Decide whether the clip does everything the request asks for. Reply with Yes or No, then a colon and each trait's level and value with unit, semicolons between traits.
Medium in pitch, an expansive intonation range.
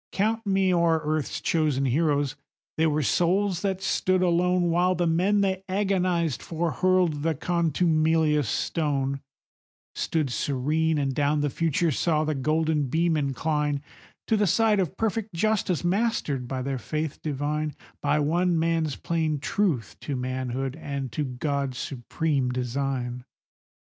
No: medium, 155 Hz; average, 4.0 semitones